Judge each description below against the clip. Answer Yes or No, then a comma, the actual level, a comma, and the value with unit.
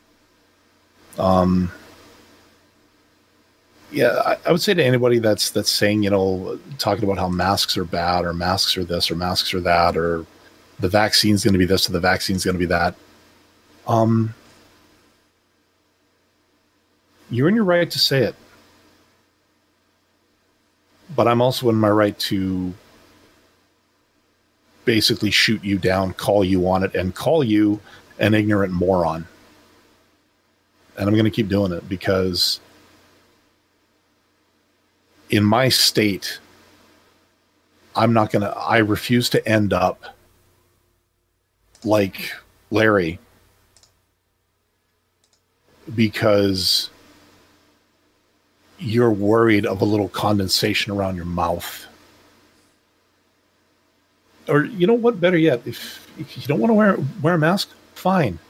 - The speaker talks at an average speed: No, slow, 120 wpm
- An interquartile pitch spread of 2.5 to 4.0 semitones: Yes, average, 3.7 semitones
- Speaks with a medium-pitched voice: No, low, 100 Hz